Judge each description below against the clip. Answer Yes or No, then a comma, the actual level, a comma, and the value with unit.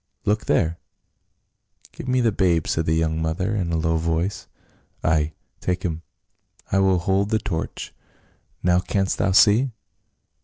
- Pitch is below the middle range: Yes, very low, 90 Hz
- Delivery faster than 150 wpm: Yes, average, 160 wpm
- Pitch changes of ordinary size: Yes, average, 3.6 semitones